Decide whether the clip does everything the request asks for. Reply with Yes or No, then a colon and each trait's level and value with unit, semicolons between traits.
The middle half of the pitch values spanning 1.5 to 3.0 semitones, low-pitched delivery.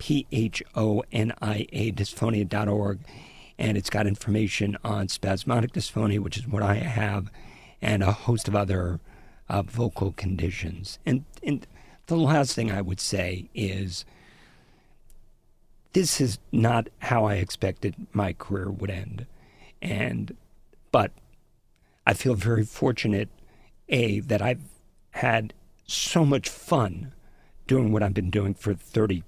Yes: average, 2.7 semitones; low, 105 Hz